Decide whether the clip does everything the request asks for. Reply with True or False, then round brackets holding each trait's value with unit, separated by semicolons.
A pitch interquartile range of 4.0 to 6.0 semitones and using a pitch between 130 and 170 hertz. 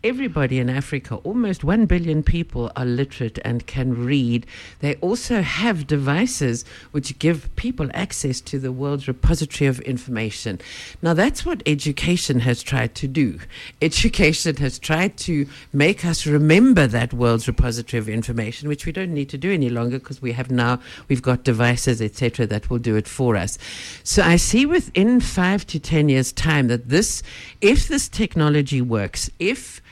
True (5.3 semitones; 140 Hz)